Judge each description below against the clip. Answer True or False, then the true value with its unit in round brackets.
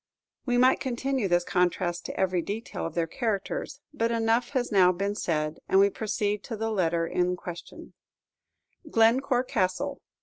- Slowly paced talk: False (160 wpm)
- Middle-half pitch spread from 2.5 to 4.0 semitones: False (4.9 semitones)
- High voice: True (205 Hz)